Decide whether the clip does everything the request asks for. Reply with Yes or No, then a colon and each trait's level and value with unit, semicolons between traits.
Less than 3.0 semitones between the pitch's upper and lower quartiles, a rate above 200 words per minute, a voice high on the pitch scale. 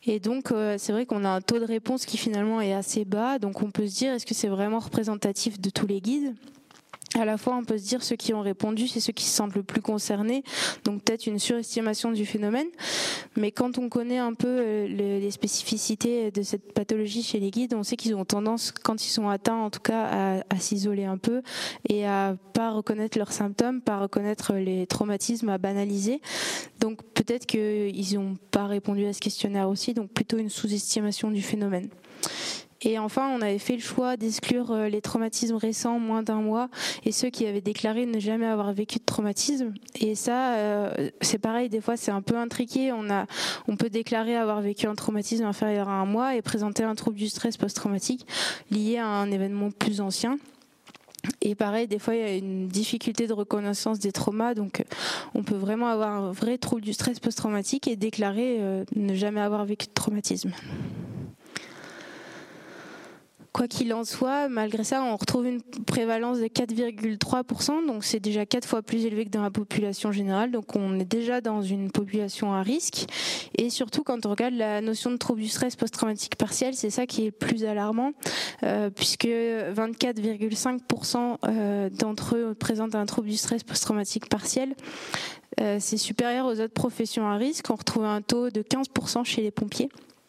No: narrow, 2.5 semitones; average, 190 wpm; high, 225 Hz